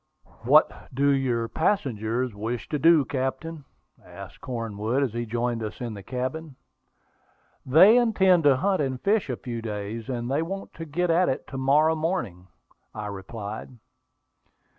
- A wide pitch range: Yes, wide, 5.8 semitones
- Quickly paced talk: No, average, 155 wpm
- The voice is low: Yes, low, 130 Hz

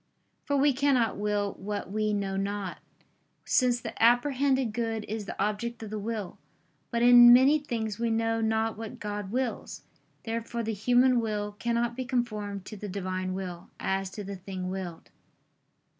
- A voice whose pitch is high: Yes, high, 220 Hz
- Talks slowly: No, average, 165 wpm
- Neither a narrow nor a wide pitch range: Yes, average, 3.0 semitones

